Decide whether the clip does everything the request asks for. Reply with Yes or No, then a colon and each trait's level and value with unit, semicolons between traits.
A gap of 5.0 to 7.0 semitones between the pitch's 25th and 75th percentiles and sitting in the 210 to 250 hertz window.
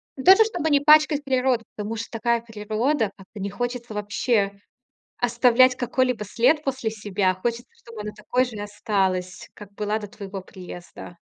No: average, 3.6 semitones; high, 225 Hz